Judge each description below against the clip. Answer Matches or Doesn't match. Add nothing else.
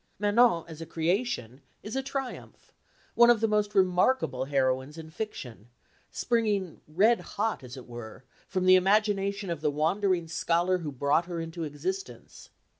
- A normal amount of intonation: Doesn't match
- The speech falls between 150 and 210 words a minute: Matches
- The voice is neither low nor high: Matches